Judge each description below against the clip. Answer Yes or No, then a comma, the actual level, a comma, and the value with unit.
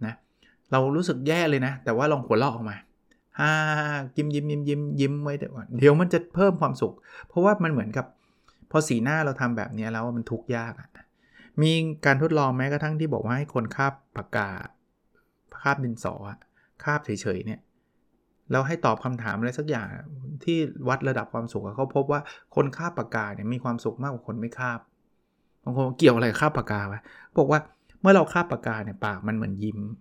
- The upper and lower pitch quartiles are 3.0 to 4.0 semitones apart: No, average, 4.6 semitones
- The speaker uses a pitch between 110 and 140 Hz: Yes, low, 135 Hz